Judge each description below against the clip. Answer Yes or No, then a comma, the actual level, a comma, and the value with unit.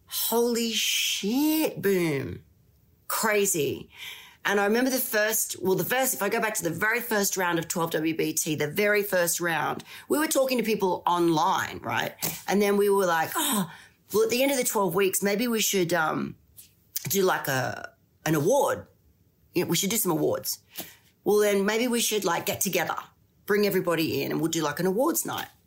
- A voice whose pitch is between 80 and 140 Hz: No, high, 200 Hz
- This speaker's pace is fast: No, average, 190 wpm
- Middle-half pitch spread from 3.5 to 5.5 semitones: Yes, average, 4.9 semitones